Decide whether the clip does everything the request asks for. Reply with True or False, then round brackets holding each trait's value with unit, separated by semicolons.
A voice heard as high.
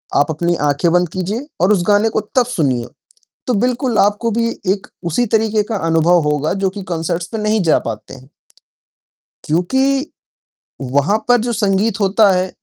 True (195 Hz)